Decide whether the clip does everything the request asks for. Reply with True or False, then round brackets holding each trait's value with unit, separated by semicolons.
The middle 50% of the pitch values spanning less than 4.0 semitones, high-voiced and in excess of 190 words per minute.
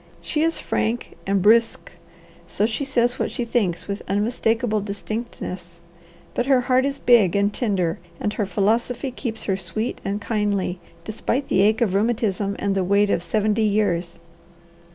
False (3.1 semitones; 210 Hz; 160 wpm)